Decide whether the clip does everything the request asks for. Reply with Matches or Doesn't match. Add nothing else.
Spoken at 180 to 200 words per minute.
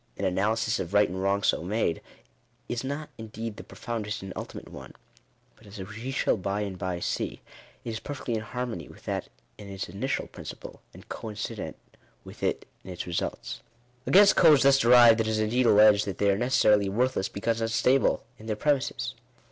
Matches